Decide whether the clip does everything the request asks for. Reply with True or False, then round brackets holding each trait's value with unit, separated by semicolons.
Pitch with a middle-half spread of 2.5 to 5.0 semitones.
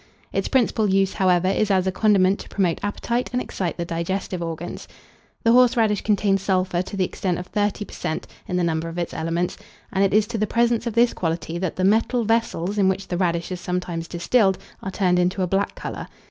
True (2.9 semitones)